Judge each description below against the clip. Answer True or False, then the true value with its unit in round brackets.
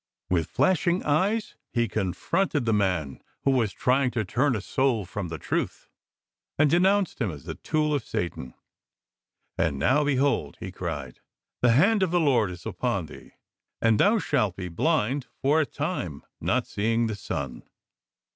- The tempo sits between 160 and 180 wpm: True (165 wpm)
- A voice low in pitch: True (120 Hz)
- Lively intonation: True (8.2 semitones)